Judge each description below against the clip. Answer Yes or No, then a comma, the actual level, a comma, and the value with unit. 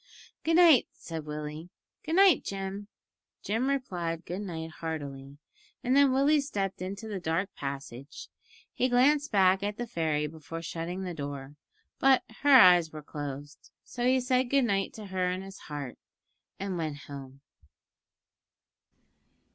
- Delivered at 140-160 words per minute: Yes, average, 145 wpm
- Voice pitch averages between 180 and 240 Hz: Yes, medium, 185 Hz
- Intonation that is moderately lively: No, wide, 8.1 semitones